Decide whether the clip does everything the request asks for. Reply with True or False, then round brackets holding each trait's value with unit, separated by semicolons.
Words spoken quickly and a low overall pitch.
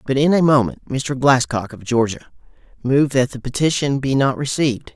False (180 wpm; 130 Hz)